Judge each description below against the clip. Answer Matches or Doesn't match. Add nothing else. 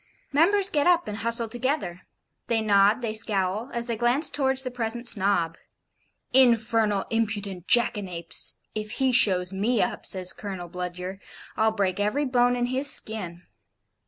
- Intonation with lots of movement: Doesn't match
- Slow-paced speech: Doesn't match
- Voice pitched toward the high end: Matches